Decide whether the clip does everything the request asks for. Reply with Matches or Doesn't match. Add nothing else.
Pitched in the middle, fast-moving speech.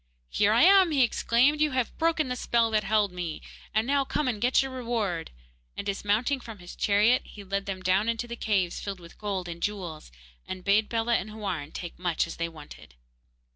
Doesn't match